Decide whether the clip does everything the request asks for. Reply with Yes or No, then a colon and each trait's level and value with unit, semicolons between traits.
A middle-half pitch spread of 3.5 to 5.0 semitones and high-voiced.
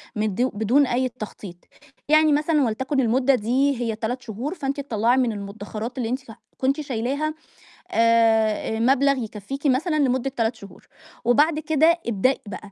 Yes: average, 3.9 semitones; very high, 250 Hz